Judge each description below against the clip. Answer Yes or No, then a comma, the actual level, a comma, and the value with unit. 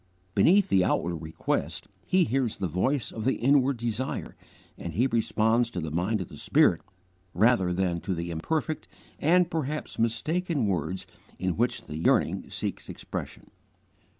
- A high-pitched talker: No, low, 110 Hz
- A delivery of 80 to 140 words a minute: No, average, 150 wpm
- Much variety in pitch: Yes, wide, 7.3 semitones